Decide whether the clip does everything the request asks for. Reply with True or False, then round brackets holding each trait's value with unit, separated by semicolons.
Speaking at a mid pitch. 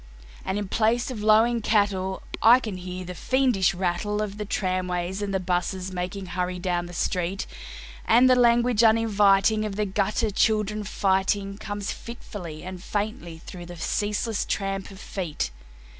False (195 Hz)